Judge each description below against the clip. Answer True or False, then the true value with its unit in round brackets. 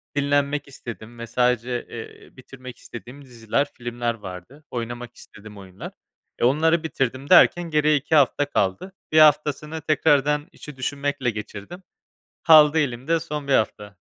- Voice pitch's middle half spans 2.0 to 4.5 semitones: True (4.0 semitones)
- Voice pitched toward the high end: False (135 Hz)